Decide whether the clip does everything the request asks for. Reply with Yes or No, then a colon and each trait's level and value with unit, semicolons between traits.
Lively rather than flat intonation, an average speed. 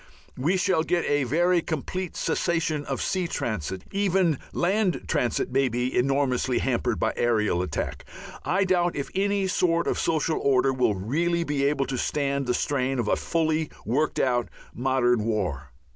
Yes: wide, 5.7 semitones; average, 160 wpm